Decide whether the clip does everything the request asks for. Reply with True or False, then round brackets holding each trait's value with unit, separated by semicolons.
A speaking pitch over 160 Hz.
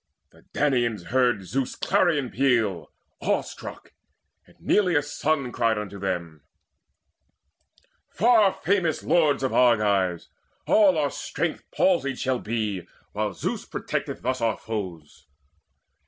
False (120 Hz)